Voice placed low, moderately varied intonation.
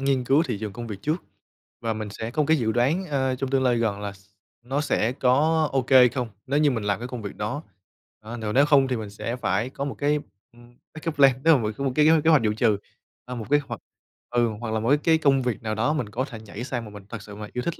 Yes: low, 125 Hz; average, 4.3 semitones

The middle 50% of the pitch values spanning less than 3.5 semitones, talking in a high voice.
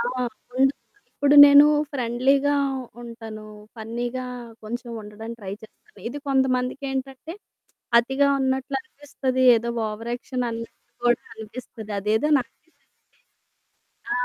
Yes: average, 2.8 semitones; very high, 250 Hz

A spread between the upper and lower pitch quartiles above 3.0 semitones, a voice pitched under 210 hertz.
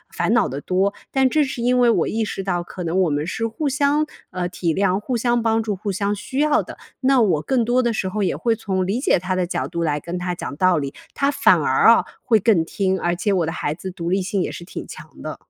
Yes: average, 5.0 semitones; high, 195 Hz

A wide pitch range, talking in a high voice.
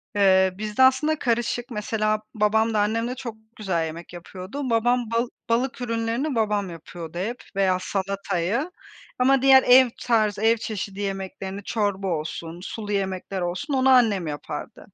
No: average, 4.0 semitones; high, 215 Hz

